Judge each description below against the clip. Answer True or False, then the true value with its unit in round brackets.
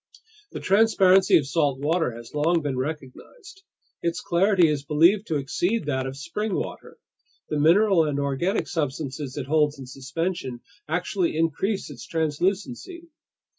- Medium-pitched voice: True (160 Hz)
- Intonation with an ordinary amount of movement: True (5.0 semitones)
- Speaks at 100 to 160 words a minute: True (140 wpm)